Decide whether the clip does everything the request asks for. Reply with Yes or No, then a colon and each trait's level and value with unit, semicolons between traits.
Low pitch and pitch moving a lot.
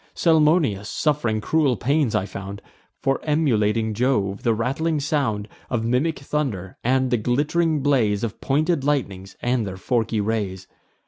Yes: low, 125 Hz; wide, 5.8 semitones